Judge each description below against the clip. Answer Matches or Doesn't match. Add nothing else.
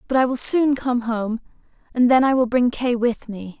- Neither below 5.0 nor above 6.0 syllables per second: Doesn't match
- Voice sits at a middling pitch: Doesn't match